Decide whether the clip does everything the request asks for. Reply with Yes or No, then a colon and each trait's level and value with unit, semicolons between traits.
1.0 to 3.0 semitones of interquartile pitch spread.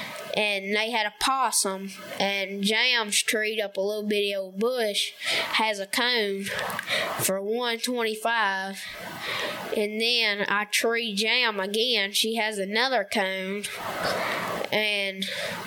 Yes: narrow, 2.6 semitones